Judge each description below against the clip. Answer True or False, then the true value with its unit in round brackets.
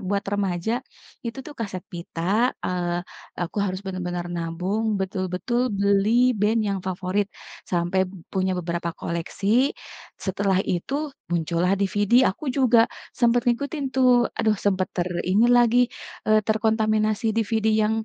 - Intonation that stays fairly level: False (3.5 semitones)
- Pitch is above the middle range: True (200 Hz)